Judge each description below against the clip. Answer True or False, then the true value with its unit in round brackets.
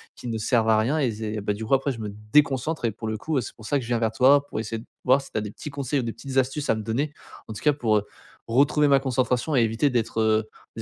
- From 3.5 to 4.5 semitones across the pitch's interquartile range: True (3.8 semitones)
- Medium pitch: False (120 Hz)